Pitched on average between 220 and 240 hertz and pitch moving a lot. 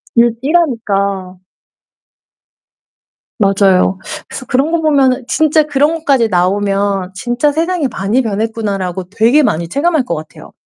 Yes: high, 230 Hz; wide, 6.5 semitones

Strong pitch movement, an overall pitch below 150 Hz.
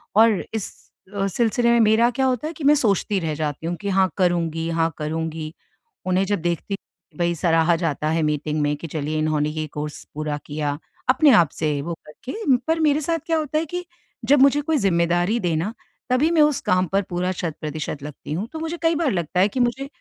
No: wide, 8.4 semitones; medium, 180 Hz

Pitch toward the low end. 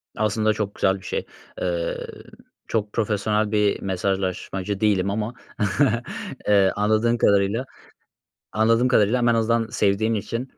Yes: low, 105 Hz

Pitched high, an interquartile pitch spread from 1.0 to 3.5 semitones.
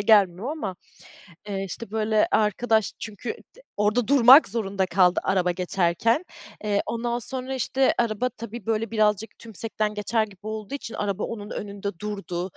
Yes: high, 215 Hz; average, 2.7 semitones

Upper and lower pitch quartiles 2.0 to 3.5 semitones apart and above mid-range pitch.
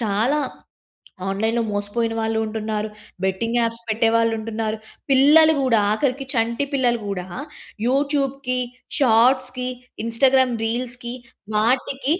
Yes: average, 2.9 semitones; high, 235 Hz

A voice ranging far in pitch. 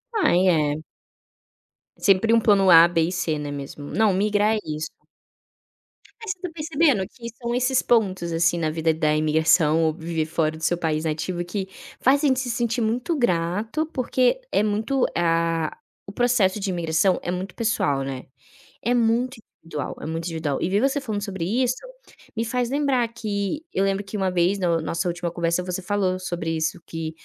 Yes: wide, 6.0 semitones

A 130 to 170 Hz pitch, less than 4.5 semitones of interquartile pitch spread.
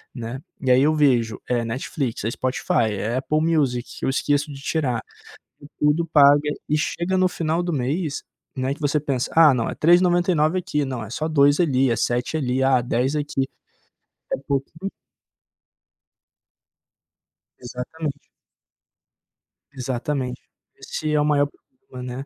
Yes: medium, 140 Hz; average, 3.6 semitones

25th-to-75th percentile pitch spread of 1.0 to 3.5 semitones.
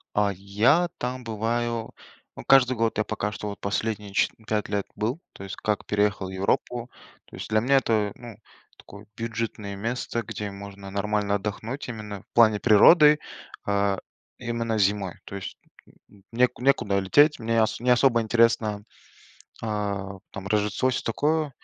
Yes: average, 2.7 semitones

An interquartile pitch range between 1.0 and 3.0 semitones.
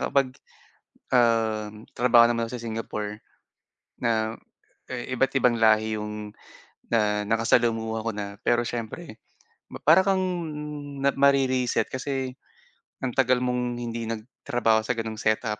Yes: narrow, 2.5 semitones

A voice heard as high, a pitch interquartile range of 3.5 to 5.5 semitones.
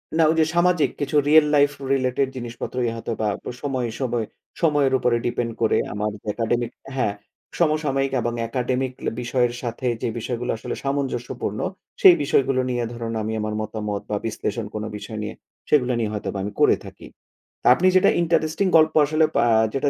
No: low, 125 Hz; average, 3.8 semitones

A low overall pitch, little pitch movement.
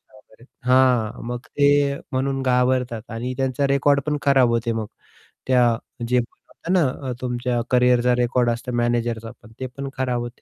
Yes: low, 125 Hz; narrow, 1.8 semitones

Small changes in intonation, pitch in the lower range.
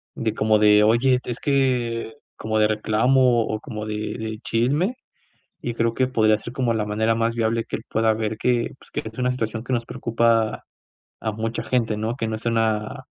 Yes: narrow, 1.7 semitones; low, 115 Hz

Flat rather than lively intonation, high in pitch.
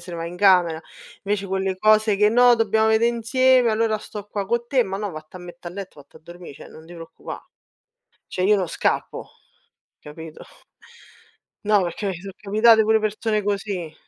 No: average, 3.7 semitones; high, 200 Hz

